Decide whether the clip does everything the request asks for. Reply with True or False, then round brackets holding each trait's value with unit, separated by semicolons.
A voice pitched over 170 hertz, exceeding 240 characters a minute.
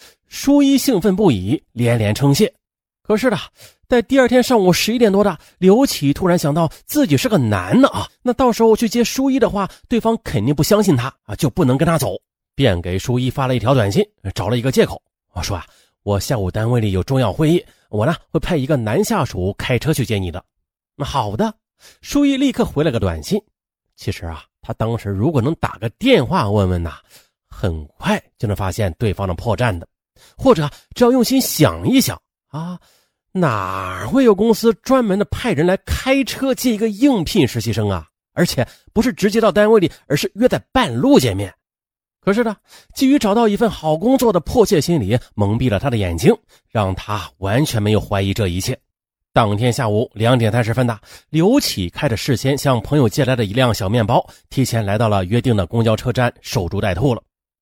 False (135 Hz; 290 characters per minute)